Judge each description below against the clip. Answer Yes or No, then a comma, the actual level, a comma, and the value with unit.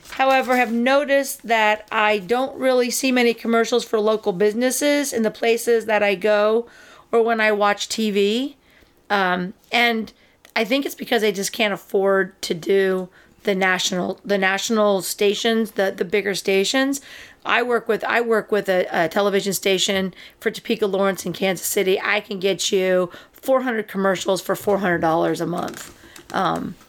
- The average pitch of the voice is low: No, high, 210 Hz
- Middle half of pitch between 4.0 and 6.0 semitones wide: No, average, 3.2 semitones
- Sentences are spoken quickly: No, average, 165 wpm